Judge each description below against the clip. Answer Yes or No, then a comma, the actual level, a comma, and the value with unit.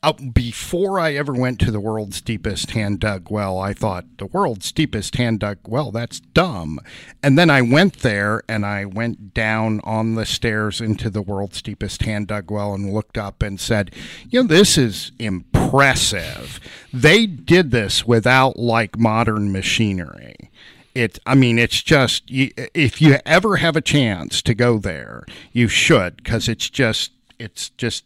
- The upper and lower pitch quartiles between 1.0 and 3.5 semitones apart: No, average, 4.0 semitones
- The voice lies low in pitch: Yes, low, 115 Hz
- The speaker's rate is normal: Yes, average, 170 wpm